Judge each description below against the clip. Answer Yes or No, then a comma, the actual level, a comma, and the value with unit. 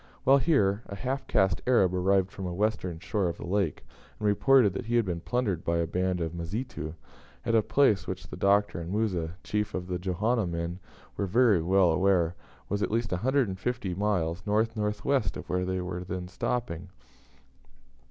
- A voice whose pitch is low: Yes, very low, 95 Hz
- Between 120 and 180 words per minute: No, average, 190 wpm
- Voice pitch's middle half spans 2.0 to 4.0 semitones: Yes, average, 3.7 semitones